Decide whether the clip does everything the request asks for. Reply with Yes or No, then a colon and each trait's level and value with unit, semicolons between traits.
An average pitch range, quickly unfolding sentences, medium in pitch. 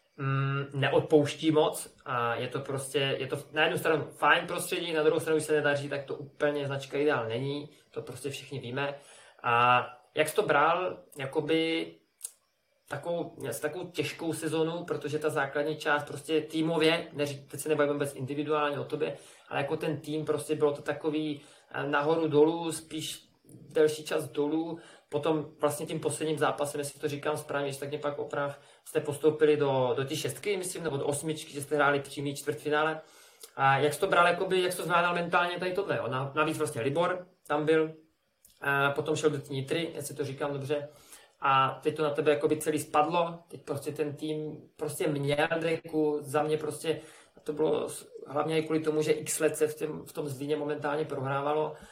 No: narrow, 1.4 semitones; fast, 185 wpm; medium, 150 Hz